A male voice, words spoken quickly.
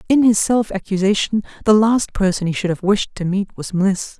No: female; fast, 215 wpm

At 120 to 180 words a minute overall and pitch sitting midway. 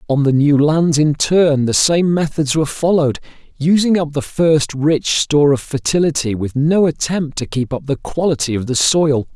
No: average, 190 wpm; medium, 150 Hz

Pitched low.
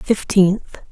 No: high, 195 Hz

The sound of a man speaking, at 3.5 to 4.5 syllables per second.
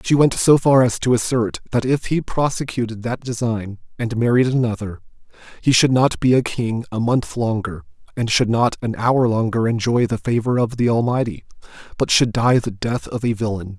No: male; 5.1 syllables/s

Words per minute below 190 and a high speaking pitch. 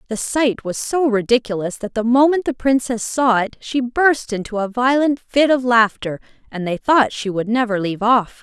No: average, 200 wpm; high, 240 Hz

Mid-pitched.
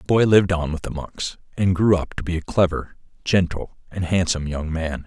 No: very low, 85 Hz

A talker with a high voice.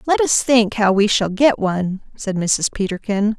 Yes: high, 210 Hz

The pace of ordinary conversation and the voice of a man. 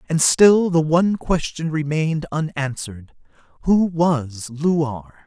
No: slow, 115 wpm; male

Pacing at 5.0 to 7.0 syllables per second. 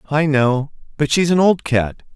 No: 4.4 syllables/s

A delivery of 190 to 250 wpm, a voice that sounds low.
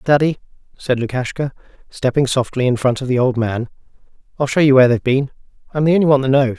Yes: average, 200 wpm; low, 130 Hz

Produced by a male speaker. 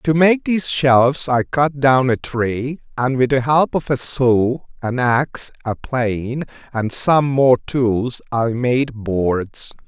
Yes: male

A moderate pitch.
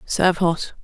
Yes: medium, 175 Hz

